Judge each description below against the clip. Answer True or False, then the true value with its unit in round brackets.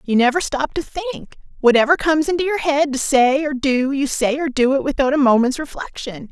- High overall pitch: True (275 Hz)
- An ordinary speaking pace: False (210 wpm)